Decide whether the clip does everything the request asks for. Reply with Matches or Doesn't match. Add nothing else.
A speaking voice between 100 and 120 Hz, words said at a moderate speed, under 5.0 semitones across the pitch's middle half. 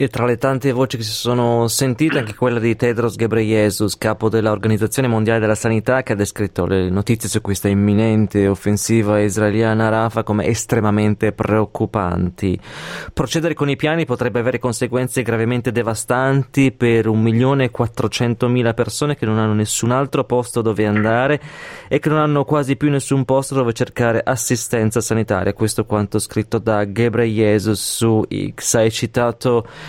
Matches